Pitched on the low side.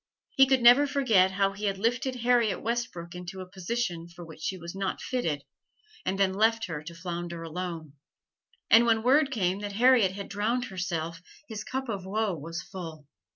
No: high, 195 Hz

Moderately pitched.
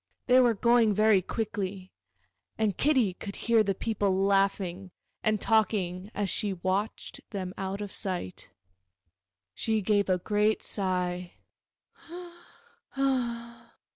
No: high, 200 Hz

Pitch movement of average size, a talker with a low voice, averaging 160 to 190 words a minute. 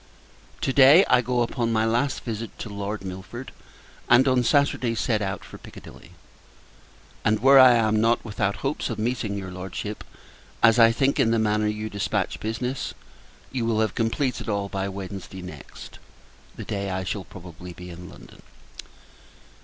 Yes: average, 3.5 semitones; low, 110 Hz; average, 165 wpm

